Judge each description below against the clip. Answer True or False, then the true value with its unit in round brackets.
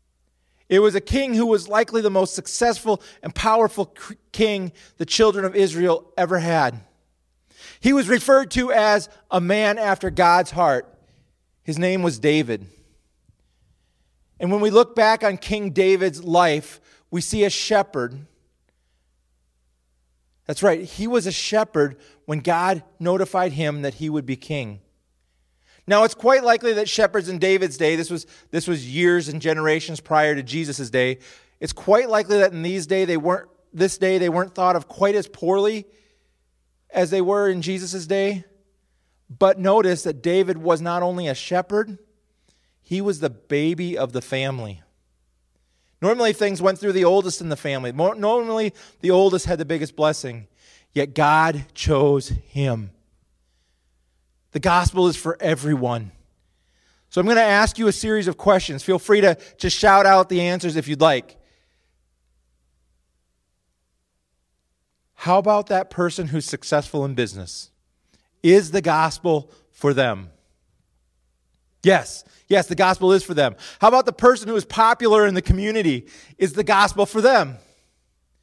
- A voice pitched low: False (170 Hz)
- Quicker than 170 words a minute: False (155 wpm)